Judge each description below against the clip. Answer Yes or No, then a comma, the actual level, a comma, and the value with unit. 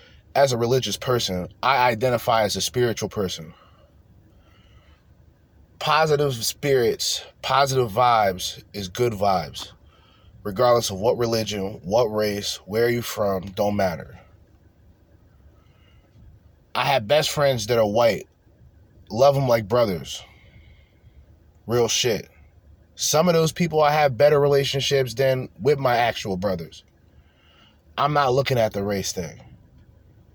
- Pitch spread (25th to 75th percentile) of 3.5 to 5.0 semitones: No, wide, 5.6 semitones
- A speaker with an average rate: No, slow, 125 wpm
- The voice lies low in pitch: Yes, low, 105 Hz